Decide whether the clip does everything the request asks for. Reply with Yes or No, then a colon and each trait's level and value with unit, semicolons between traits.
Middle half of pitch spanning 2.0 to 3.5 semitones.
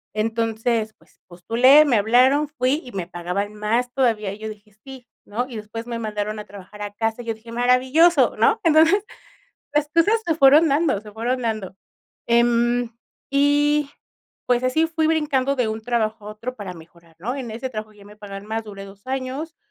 No: average, 4.3 semitones